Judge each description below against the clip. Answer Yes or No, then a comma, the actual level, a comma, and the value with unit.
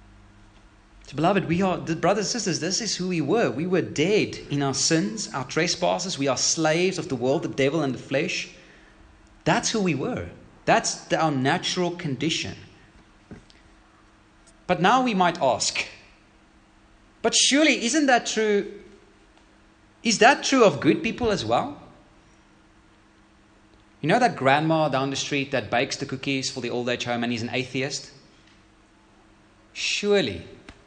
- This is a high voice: No, medium, 140 Hz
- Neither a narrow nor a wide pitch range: No, wide, 8.9 semitones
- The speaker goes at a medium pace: Yes, average, 155 wpm